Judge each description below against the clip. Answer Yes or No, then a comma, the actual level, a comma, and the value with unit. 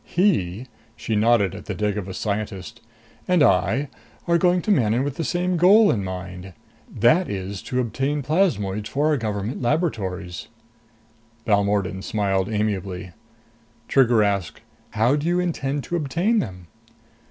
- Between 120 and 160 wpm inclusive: Yes, average, 140 wpm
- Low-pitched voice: Yes, low, 110 Hz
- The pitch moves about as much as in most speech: No, wide, 7.3 semitones